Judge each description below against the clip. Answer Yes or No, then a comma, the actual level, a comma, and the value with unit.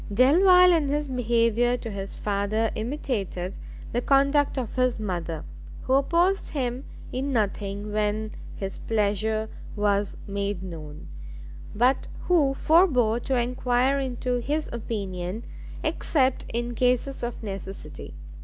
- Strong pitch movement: No, average, 4.7 semitones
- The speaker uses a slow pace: Yes, slow, 120 wpm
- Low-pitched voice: No, high, 235 Hz